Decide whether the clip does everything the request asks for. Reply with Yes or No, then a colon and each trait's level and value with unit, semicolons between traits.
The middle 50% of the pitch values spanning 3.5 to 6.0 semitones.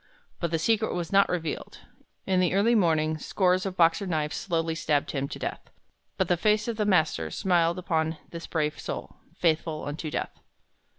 No: average, 3.0 semitones